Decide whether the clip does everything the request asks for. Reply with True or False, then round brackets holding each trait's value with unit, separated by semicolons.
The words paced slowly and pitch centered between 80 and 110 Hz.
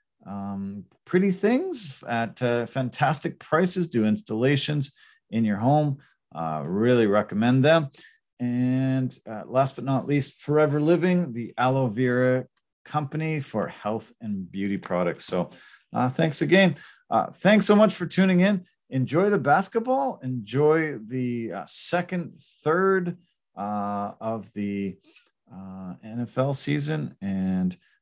False (125 wpm; 135 Hz)